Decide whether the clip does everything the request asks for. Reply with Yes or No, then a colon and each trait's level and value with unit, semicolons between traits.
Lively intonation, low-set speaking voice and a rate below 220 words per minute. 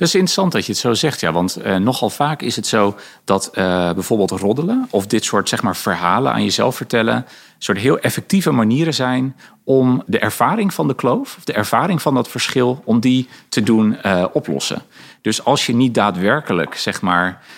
Yes: wide, 6.5 semitones; low, 125 Hz; fast, 200 wpm